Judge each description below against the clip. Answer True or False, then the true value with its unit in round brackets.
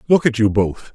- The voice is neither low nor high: False (120 Hz)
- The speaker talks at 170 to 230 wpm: False (255 wpm)